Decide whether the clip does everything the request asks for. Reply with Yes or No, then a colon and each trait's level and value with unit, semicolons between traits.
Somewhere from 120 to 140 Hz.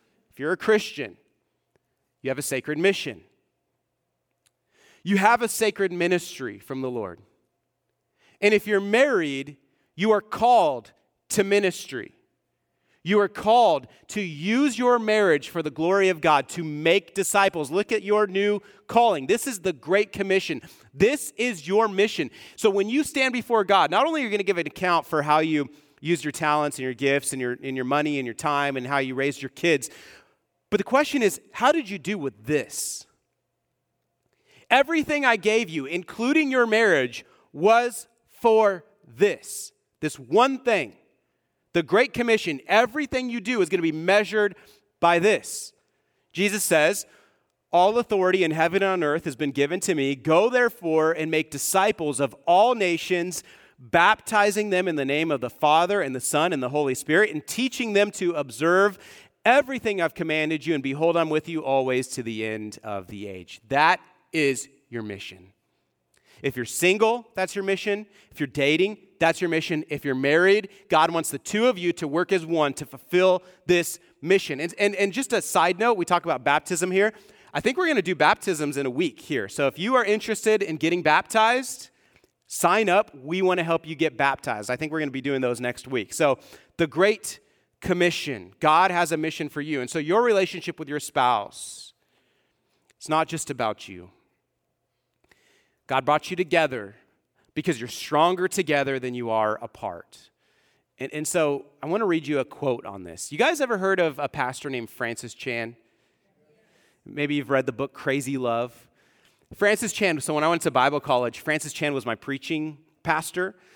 No: medium, 165 Hz